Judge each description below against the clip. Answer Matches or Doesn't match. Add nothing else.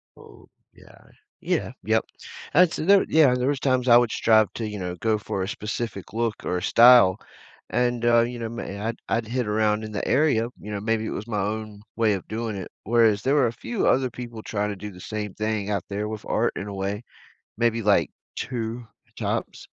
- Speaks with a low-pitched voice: Matches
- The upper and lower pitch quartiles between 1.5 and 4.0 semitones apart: Matches